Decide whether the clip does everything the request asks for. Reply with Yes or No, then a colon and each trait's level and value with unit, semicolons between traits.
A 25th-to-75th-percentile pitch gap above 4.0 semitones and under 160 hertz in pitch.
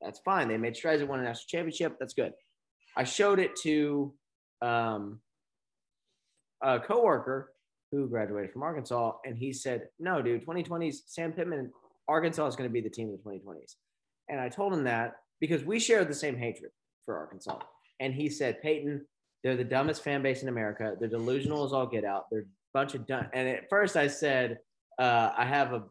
Yes: average, 4.6 semitones; low, 135 Hz